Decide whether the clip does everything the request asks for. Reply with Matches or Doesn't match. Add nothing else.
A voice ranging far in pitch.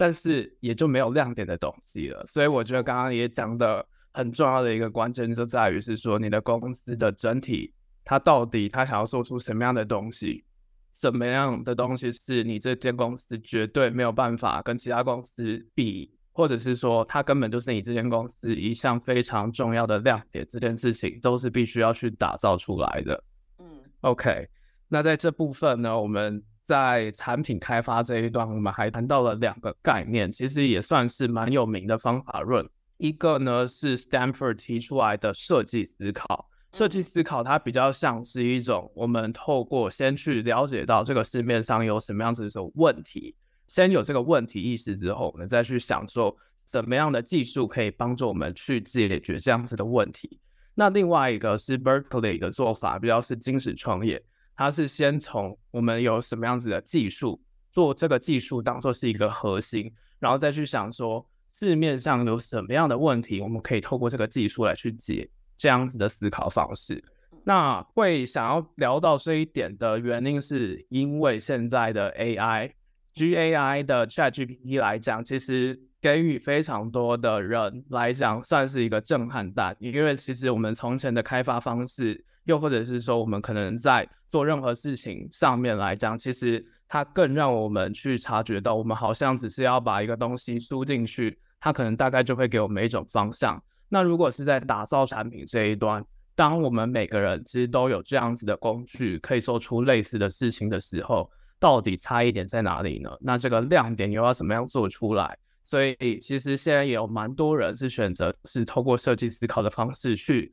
Doesn't match